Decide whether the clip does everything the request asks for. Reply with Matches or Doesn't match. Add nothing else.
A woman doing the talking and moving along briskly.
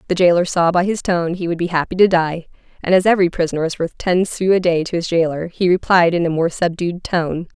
Matches